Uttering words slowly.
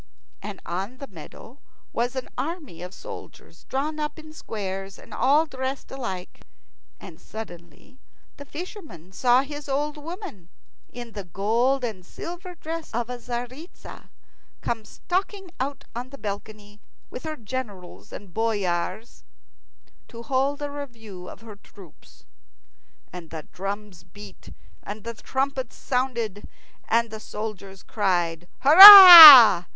Yes: slow, 130 wpm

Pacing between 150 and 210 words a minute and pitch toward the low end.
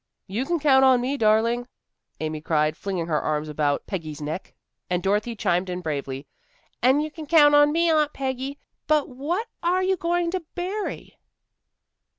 No: average, 170 wpm; very high, 250 Hz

